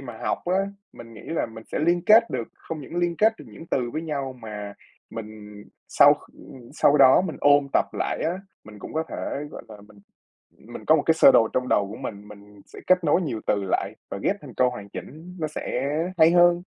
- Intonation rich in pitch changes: Yes, wide, 7.0 semitones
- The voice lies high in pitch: No, low, 130 Hz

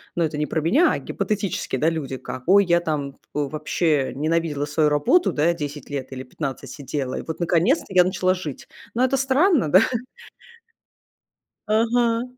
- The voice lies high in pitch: No, medium, 160 Hz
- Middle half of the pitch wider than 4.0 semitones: Yes, wide, 5.5 semitones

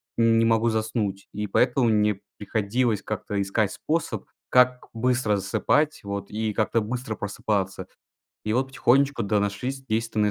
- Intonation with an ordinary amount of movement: Yes, average, 3.3 semitones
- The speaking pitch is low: Yes, low, 110 Hz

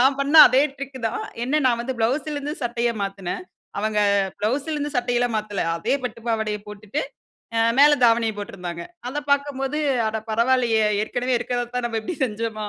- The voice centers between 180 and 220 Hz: No, high, 240 Hz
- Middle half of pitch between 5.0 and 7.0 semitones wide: No, average, 3.9 semitones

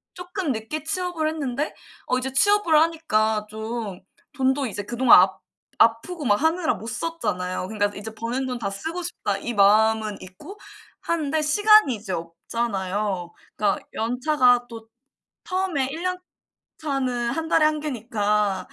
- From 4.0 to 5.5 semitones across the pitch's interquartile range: No, wide, 6.8 semitones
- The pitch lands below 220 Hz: No, high, 245 Hz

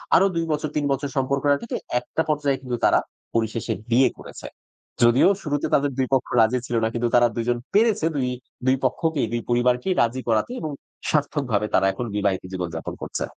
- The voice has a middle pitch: No, low, 130 Hz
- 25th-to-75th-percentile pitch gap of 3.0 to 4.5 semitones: Yes, average, 3.7 semitones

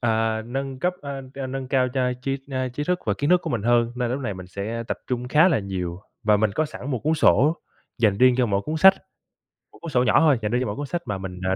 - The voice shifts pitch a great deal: No, average, 4.3 semitones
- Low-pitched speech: Yes, low, 125 Hz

